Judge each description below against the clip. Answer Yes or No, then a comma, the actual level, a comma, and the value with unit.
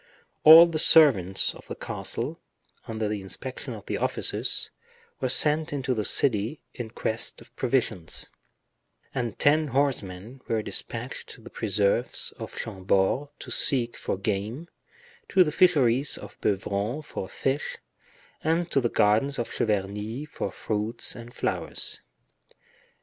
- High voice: No, low, 120 Hz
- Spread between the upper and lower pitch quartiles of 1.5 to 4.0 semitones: No, average, 5.3 semitones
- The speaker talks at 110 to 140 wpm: Yes, slow, 135 wpm